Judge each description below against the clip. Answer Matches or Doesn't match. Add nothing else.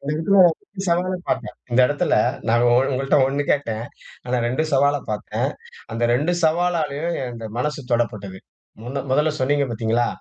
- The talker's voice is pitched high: Doesn't match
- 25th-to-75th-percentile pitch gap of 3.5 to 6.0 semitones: Matches